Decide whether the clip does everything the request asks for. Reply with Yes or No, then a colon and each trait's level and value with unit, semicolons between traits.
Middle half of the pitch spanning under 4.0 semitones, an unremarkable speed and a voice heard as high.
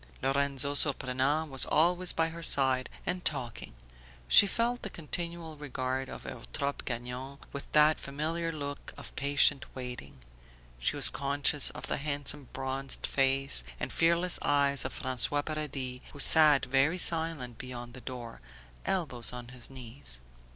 No: average, 3.2 semitones; average, 145 wpm; medium, 140 Hz